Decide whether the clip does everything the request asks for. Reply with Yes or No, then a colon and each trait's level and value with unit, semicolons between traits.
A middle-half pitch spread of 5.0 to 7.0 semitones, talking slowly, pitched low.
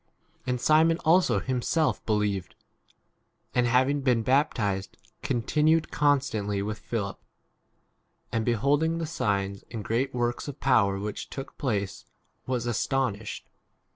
Yes: average, 5.3 semitones; slow, 130 wpm; low, 120 Hz